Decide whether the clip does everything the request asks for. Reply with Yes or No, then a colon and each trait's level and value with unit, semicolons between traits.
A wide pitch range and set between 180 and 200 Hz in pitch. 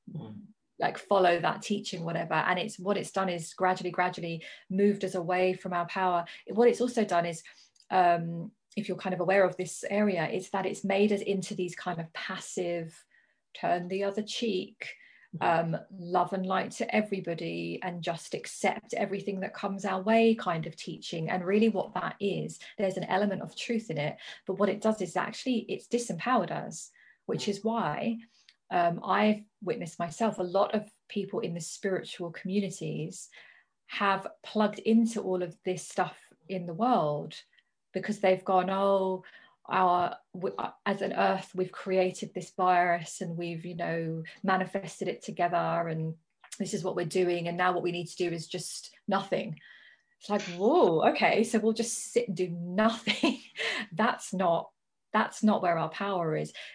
No: average, 3.0 semitones; high, 190 Hz